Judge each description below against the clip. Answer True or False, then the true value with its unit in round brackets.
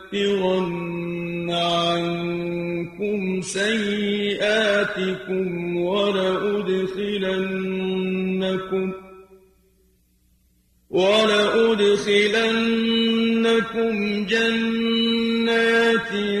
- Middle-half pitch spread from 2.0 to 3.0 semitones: True (2.5 semitones)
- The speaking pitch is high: True (195 Hz)